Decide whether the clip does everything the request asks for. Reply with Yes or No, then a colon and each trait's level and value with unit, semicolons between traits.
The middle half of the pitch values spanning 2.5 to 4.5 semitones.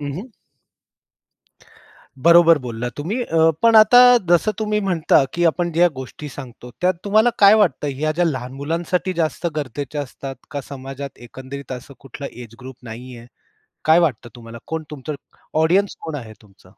No: average, 4.9 semitones